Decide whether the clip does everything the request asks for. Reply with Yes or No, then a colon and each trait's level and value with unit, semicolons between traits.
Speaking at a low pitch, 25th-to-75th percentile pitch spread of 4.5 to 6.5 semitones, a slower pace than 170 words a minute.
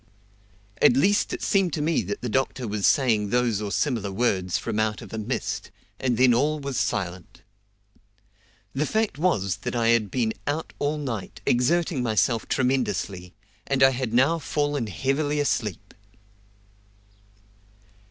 Yes: low, 125 Hz; average, 5.2 semitones; average, 150 wpm